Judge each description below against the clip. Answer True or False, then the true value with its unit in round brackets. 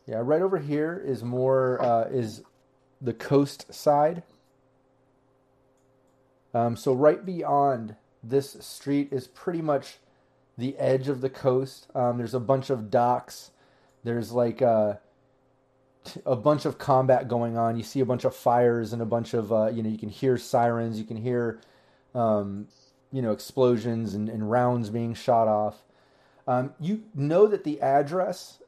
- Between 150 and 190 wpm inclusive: True (160 wpm)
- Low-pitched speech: True (130 Hz)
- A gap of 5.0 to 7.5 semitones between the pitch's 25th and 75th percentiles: False (2.5 semitones)